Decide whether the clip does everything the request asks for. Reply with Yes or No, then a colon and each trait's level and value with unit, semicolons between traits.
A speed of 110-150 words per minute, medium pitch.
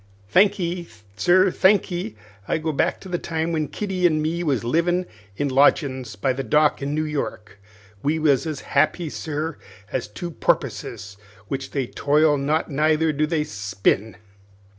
No: average, 160 wpm; medium, 155 Hz